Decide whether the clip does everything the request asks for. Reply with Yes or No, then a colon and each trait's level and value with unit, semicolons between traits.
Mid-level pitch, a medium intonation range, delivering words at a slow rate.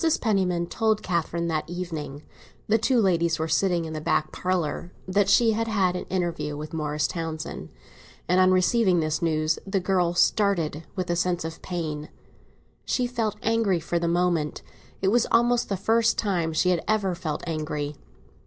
No: medium, 175 Hz; average, 3.7 semitones; average, 165 wpm